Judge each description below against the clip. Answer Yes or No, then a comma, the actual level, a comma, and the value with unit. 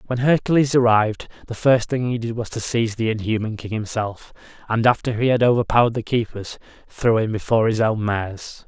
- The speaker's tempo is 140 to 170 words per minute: No, average, 195 wpm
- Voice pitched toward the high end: No, low, 115 Hz